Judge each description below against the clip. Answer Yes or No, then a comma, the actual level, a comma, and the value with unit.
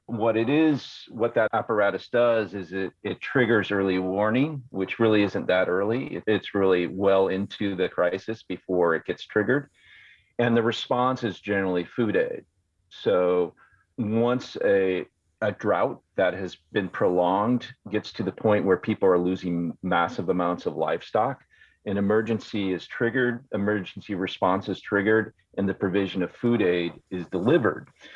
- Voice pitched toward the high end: No, low, 100 Hz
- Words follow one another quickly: No, average, 155 wpm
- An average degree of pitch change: Yes, average, 3.5 semitones